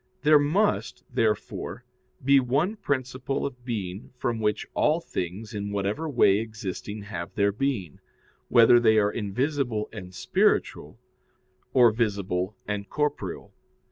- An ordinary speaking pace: No, slow, 125 wpm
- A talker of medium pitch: No, low, 110 Hz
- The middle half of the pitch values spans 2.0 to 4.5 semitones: No, average, 5.0 semitones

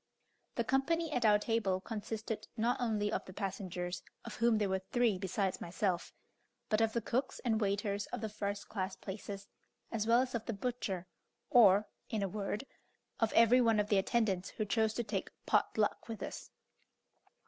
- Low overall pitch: No, high, 215 Hz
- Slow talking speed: No, average, 180 wpm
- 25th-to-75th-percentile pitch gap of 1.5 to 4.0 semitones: Yes, average, 2.7 semitones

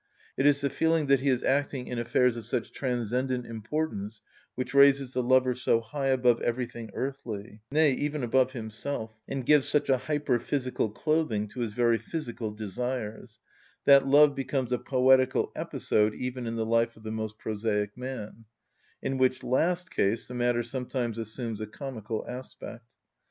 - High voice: No, low, 125 Hz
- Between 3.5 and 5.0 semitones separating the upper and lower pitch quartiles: No, average, 3.0 semitones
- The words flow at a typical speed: Yes, average, 165 wpm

